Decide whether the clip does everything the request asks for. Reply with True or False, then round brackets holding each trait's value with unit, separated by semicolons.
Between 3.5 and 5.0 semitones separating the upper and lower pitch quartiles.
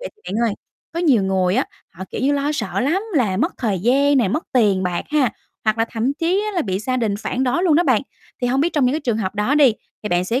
False (5.6 semitones)